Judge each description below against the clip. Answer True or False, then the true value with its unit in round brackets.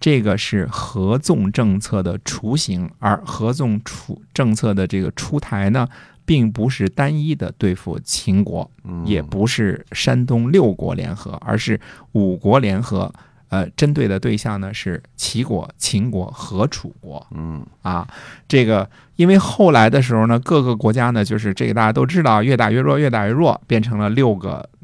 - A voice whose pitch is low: True (110 Hz)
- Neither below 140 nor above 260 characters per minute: True (245 characters per minute)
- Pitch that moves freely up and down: False (5.0 semitones)